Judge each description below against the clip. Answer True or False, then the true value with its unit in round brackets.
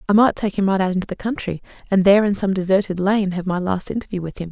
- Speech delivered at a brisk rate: True (280 wpm)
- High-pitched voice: True (195 Hz)